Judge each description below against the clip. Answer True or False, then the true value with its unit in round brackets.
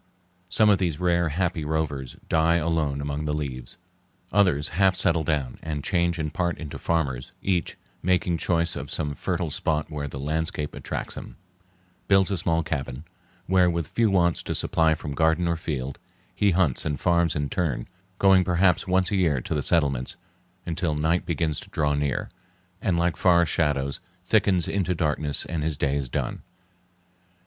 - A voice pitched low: True (80 Hz)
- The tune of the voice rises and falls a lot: False (3.3 semitones)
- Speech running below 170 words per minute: False (175 wpm)